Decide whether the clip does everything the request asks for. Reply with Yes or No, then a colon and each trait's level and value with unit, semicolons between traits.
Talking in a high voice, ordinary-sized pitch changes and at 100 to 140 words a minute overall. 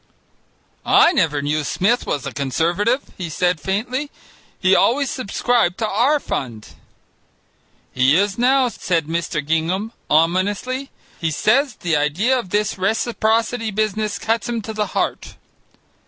No: high, 205 Hz; wide, 6.1 semitones; slow, 135 wpm